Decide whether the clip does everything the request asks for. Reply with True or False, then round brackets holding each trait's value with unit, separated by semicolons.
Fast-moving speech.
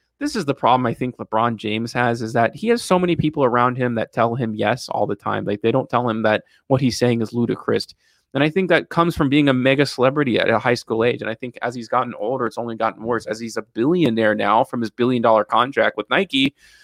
True (265 wpm)